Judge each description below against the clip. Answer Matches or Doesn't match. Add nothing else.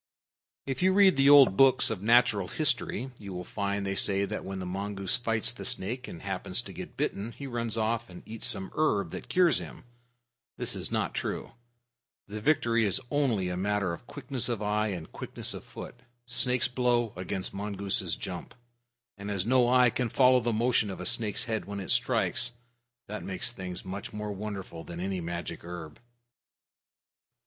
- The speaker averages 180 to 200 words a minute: Matches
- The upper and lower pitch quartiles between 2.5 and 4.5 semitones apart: Matches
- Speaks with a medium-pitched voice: Doesn't match